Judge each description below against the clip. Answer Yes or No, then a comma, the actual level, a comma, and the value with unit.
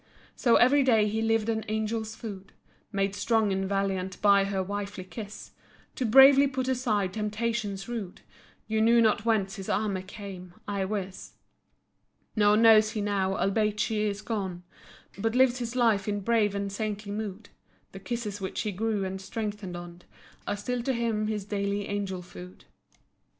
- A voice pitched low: No, high, 210 Hz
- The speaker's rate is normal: Yes, average, 165 wpm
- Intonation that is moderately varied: No, narrow, 2.3 semitones